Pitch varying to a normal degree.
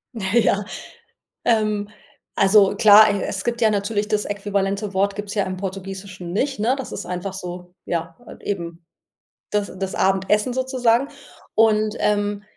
No: narrow, 2.0 semitones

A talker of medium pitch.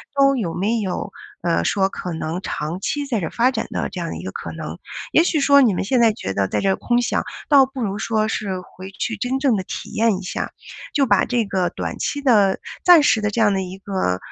No: high, 210 Hz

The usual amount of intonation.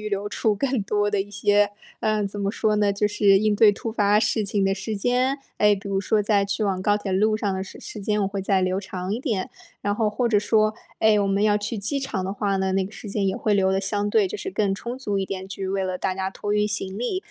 No: narrow, 1.5 semitones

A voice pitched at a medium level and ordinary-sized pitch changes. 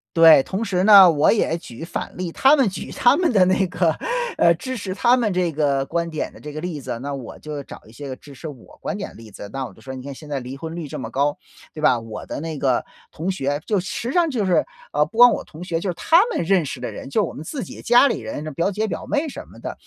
No: medium, 165 Hz; wide, 6.1 semitones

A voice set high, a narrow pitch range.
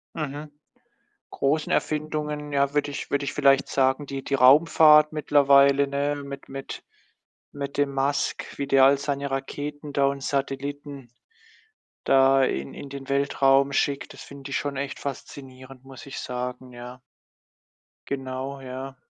No: medium, 140 Hz; narrow, 1.1 semitones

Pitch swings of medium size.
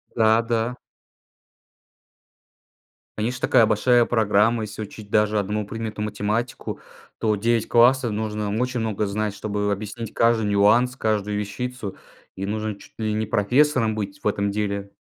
No: narrow, 2.0 semitones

